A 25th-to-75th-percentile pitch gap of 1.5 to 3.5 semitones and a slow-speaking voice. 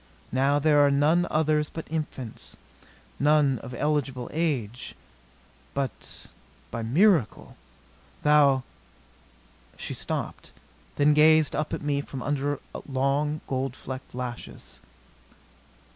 Yes: narrow, 2.6 semitones; slow, 115 wpm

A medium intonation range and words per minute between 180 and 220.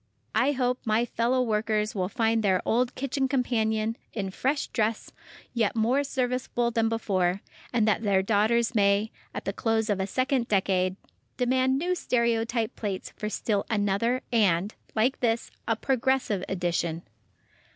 No: average, 3.4 semitones; average, 150 wpm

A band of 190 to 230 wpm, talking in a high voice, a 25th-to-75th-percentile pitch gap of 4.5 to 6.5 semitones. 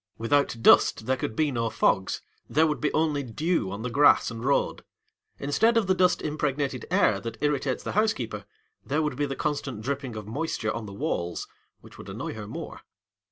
No: average, 195 wpm; low, 135 Hz; average, 5.0 semitones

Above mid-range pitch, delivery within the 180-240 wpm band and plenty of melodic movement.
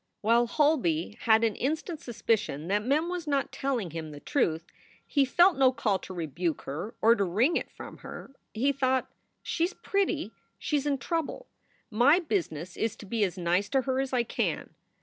Yes: high, 240 Hz; average, 190 wpm; wide, 7.0 semitones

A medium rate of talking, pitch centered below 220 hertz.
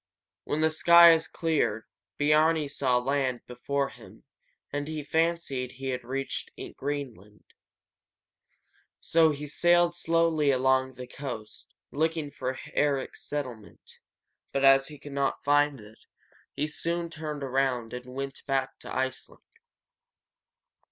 No: slow, 120 wpm; medium, 140 Hz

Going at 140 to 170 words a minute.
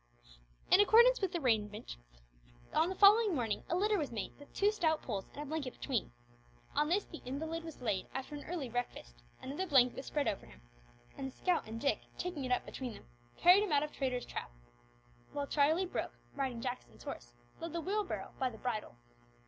No: average, 200 wpm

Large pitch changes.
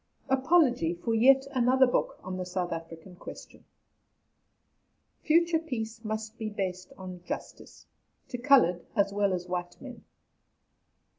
Yes: wide, 6.2 semitones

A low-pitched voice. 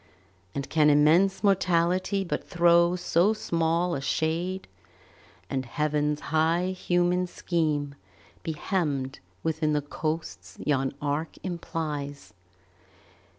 No: medium, 160 Hz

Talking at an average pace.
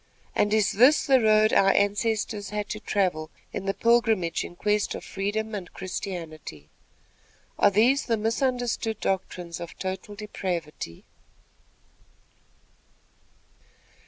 No: slow, 115 wpm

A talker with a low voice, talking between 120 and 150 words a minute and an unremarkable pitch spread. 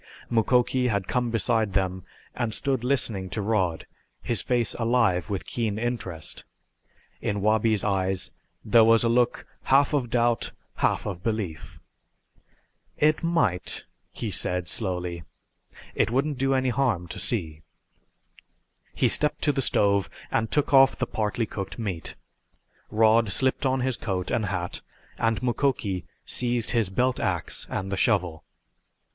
Yes: low, 110 Hz; average, 140 wpm; average, 4.4 semitones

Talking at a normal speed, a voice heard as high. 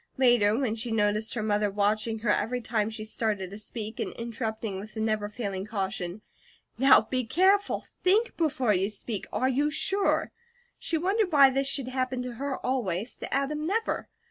Yes: average, 180 wpm; high, 230 Hz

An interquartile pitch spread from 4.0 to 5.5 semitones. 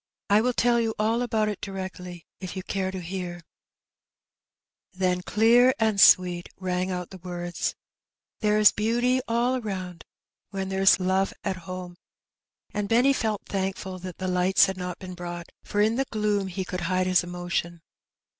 No: average, 2.8 semitones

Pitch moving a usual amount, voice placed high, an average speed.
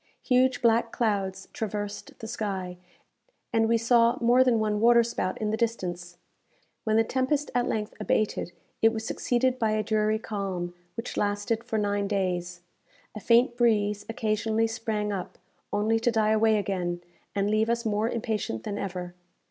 No: narrow, 2.2 semitones; high, 215 Hz; average, 165 wpm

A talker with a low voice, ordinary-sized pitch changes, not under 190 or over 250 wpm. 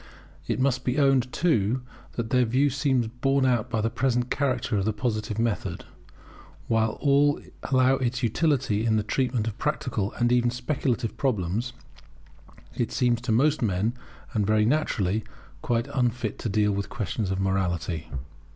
No: low, 120 Hz; average, 3.4 semitones; average, 160 wpm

